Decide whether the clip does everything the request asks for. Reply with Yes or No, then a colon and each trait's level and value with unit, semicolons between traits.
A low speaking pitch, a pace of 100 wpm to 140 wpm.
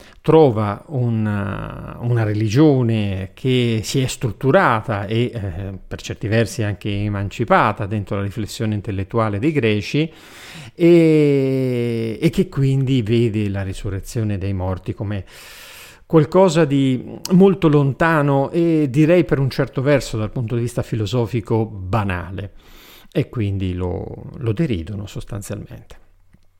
Yes: low, 115 Hz; average, 120 wpm